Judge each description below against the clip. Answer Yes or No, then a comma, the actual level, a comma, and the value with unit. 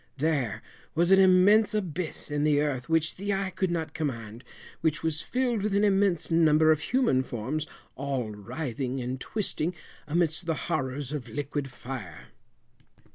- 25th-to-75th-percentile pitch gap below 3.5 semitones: No, wide, 5.6 semitones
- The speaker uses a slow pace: No, average, 155 wpm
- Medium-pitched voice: Yes, medium, 155 Hz